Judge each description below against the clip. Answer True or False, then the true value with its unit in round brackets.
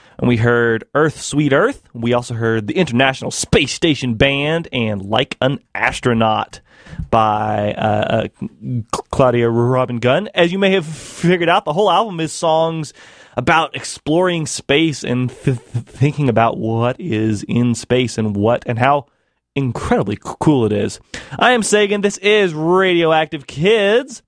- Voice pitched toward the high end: False (135 Hz)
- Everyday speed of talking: True (155 wpm)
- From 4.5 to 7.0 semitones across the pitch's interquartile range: True (5.4 semitones)